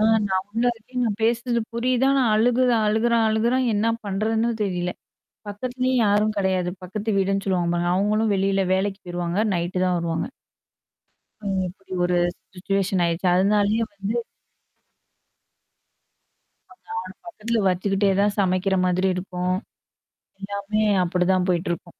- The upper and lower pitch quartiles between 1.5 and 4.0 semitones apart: Yes, average, 3.3 semitones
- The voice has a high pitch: Yes, high, 200 Hz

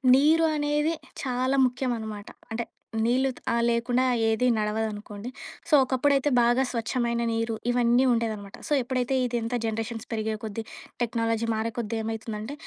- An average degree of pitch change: No, narrow, 2.3 semitones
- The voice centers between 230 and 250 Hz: Yes, high, 235 Hz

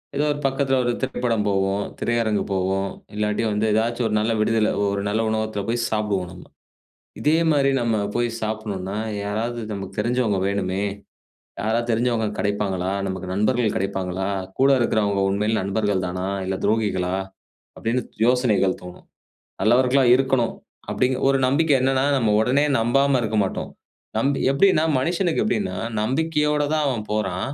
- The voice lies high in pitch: No, low, 110 Hz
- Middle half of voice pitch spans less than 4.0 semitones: No, average, 4.3 semitones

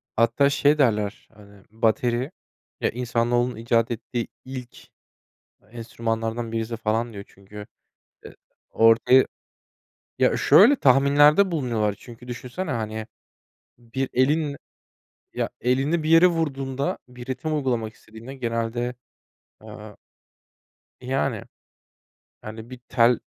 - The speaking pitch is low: Yes, low, 120 Hz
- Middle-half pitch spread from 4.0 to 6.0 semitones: No, average, 3.1 semitones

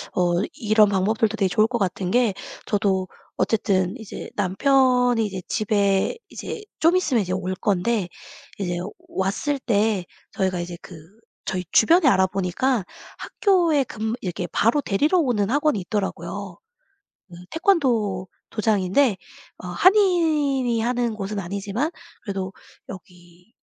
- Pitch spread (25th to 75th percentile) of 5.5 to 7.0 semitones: No, average, 5.1 semitones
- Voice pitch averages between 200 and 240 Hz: Yes, high, 210 Hz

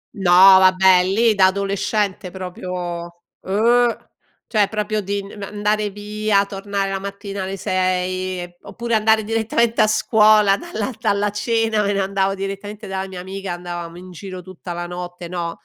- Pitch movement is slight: Yes, narrow, 2.2 semitones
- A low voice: No, high, 195 Hz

